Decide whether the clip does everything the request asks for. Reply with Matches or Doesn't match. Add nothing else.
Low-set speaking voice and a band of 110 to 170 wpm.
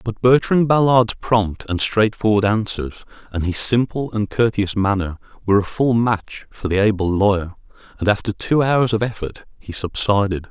Matches